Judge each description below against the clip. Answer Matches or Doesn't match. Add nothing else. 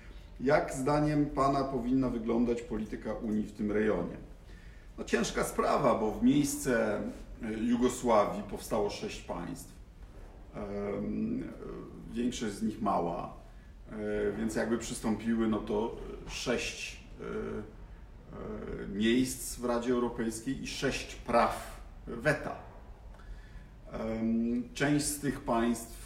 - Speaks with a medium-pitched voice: Doesn't match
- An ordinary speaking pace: Doesn't match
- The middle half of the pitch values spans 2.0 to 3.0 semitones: Matches